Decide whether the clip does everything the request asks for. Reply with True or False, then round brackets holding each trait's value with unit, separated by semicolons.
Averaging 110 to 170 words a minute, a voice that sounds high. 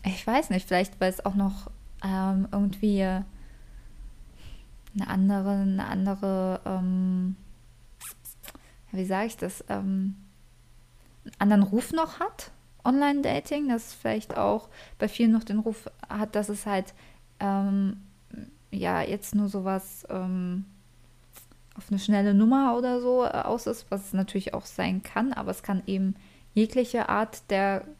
True (140 wpm; 195 Hz)